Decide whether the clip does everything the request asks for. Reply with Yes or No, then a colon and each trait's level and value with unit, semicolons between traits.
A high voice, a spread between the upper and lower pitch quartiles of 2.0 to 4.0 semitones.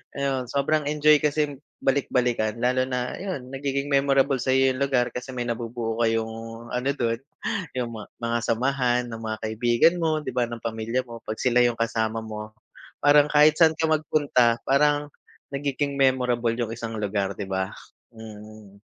No: low, 125 Hz; average, 3.4 semitones